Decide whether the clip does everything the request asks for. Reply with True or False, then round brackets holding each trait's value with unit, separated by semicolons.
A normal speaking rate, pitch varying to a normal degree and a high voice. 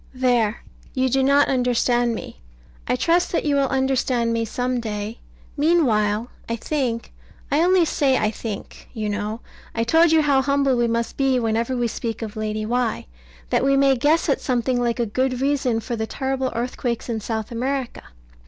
True (180 wpm; 3.0 semitones; 245 Hz)